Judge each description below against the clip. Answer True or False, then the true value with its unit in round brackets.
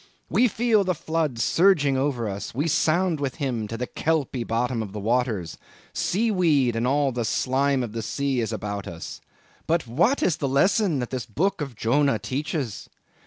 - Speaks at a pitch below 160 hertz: True (135 Hz)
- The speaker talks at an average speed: True (185 wpm)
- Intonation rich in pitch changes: True (5.8 semitones)